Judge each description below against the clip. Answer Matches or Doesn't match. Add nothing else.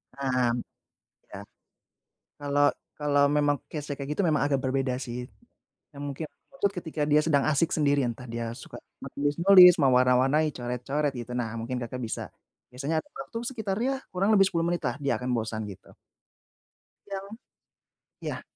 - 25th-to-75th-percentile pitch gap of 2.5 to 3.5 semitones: Doesn't match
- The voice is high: Doesn't match